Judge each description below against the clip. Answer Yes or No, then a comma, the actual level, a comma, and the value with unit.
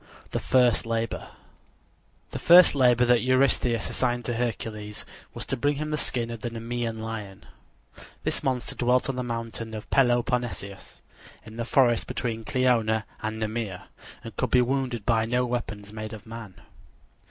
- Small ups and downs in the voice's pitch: Yes, narrow, 2.1 semitones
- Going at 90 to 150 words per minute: No, average, 160 wpm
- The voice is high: No, low, 120 Hz